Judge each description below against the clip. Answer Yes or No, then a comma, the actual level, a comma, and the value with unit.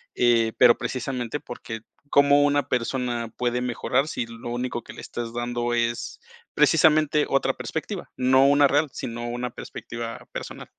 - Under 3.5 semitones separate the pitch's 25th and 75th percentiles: Yes, narrow, 2.5 semitones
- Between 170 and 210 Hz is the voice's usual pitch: No, low, 125 Hz